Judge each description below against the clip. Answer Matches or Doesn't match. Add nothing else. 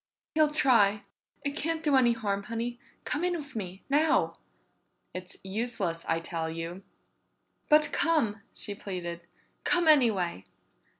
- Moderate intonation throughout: Doesn't match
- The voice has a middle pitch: Doesn't match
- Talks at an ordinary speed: Doesn't match